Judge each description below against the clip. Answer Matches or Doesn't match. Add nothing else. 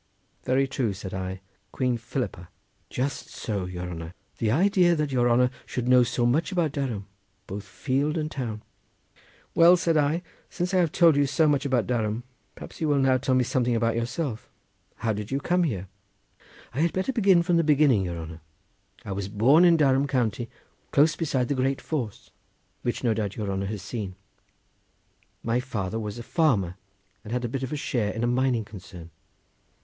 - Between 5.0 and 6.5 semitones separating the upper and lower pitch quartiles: Matches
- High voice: Doesn't match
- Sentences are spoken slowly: Doesn't match